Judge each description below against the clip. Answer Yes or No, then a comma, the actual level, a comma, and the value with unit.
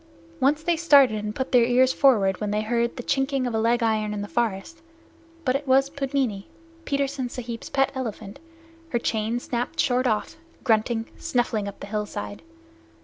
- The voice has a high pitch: Yes, high, 240 Hz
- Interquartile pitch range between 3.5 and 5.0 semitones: Yes, average, 3.8 semitones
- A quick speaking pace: No, average, 175 wpm